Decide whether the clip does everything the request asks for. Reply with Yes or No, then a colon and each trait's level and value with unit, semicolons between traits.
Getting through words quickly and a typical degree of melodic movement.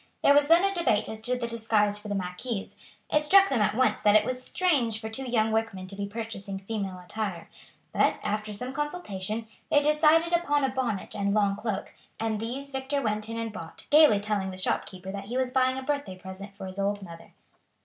Yes: fast, 215 wpm; average, 4.8 semitones